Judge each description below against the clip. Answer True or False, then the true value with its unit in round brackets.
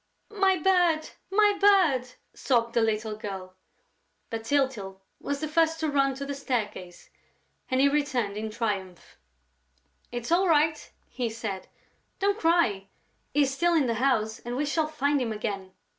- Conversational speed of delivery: True (160 wpm)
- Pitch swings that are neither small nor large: False (6.2 semitones)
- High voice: True (265 Hz)